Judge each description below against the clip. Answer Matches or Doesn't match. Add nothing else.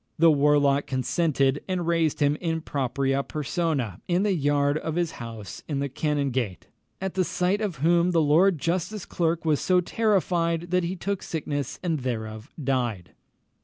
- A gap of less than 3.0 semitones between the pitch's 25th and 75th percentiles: Doesn't match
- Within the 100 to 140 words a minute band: Doesn't match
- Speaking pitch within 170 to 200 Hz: Doesn't match